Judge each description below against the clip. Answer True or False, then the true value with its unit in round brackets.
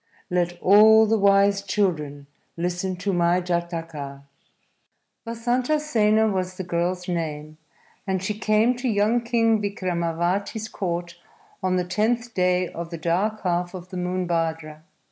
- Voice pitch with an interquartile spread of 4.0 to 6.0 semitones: False (3.6 semitones)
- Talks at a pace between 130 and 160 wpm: True (140 wpm)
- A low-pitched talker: False (185 Hz)